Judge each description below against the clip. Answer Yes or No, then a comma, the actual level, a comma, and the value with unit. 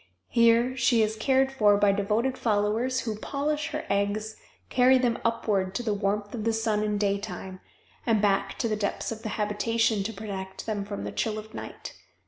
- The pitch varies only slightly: Yes, narrow, 2.3 semitones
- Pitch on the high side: Yes, high, 215 Hz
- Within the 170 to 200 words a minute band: Yes, average, 190 wpm